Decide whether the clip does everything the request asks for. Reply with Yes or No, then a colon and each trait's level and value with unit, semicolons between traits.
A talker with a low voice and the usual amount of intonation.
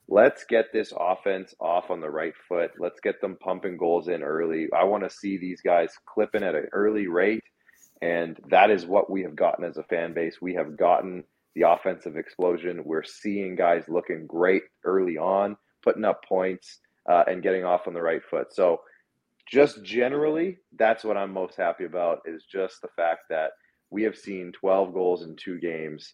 Yes: very low, 95 Hz; average, 3.9 semitones